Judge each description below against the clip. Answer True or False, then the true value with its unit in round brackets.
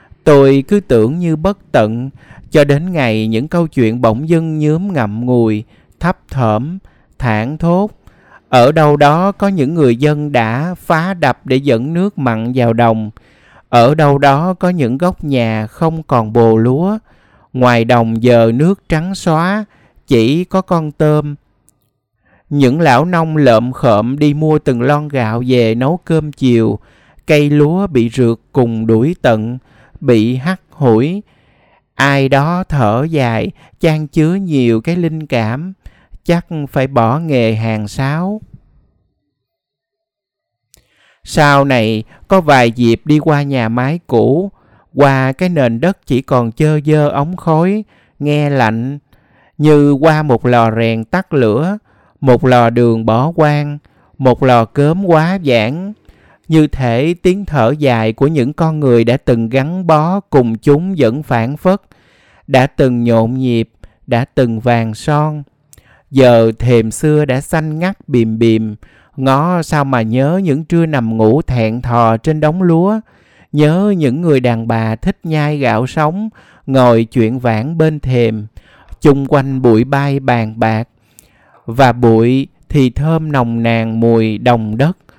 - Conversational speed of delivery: False (150 wpm)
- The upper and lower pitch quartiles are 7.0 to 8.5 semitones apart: False (5.1 semitones)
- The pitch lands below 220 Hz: True (135 Hz)